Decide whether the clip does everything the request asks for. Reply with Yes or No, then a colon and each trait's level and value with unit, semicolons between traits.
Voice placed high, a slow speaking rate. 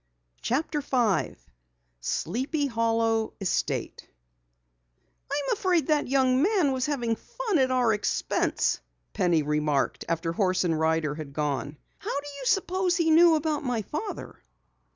Yes: very high, 250 Hz; slow, 130 wpm